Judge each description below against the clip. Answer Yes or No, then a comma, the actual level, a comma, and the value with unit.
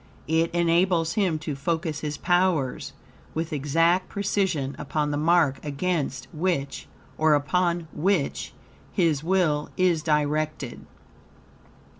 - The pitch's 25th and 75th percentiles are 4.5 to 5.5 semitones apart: No, average, 3.1 semitones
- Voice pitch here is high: No, medium, 160 Hz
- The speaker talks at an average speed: No, slow, 110 wpm